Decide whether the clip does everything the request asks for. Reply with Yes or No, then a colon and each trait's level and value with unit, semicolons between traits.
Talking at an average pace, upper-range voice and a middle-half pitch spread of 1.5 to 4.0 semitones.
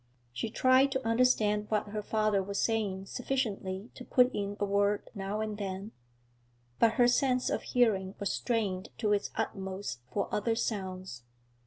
Yes: average, 160 wpm; high, 210 Hz; average, 2.7 semitones